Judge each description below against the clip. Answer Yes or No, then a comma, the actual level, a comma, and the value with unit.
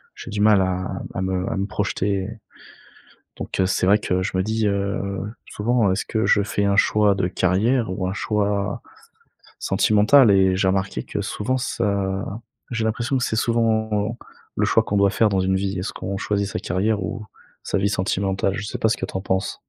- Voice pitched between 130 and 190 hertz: No, low, 100 Hz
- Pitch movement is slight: Yes, narrow, 2.2 semitones